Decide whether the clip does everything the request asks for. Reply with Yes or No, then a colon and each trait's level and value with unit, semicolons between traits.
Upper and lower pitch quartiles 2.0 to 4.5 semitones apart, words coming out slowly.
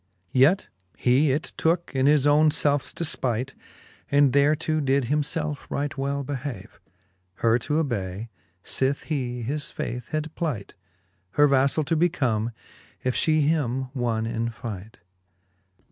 Yes: average, 3.6 semitones; slow, 130 wpm